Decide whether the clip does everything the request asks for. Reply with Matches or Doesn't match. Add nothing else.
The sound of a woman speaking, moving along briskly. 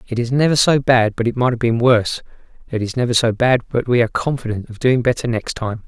Doesn't match